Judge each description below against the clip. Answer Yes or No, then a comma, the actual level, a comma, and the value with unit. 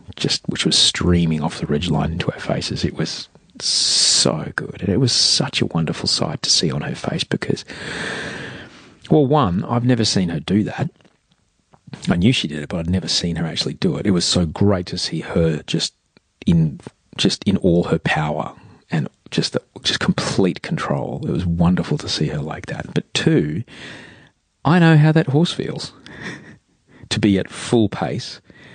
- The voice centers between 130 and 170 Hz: No, very low, 90 Hz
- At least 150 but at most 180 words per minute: No, average, 190 wpm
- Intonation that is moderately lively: No, wide, 6.4 semitones